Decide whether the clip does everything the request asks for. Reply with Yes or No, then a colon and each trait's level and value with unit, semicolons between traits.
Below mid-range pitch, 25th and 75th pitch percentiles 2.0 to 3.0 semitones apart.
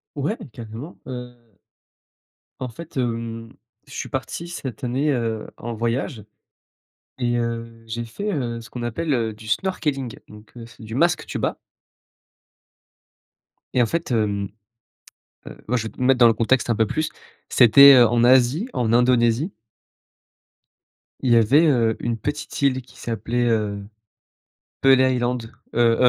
Yes: low, 120 Hz; narrow, 2.5 semitones